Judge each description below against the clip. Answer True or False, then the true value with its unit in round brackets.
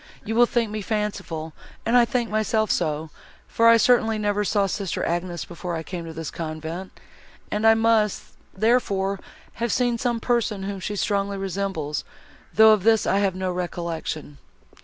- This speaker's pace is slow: False (170 wpm)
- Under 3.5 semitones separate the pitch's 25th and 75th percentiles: False (4.3 semitones)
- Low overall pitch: False (200 Hz)